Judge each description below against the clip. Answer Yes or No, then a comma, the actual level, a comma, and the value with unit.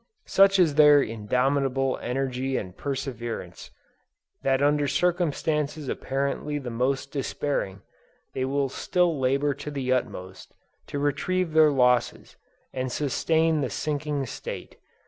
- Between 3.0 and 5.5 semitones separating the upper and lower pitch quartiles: No, narrow, 2.5 semitones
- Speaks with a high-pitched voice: No, medium, 140 Hz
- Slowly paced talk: Yes, slow, 120 wpm